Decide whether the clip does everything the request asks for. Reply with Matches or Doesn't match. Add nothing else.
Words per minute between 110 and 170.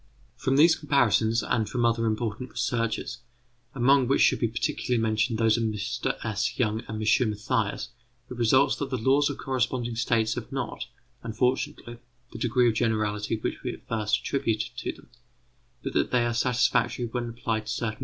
Doesn't match